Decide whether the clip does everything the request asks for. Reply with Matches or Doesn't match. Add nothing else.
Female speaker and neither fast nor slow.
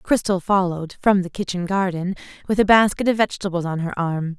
Matches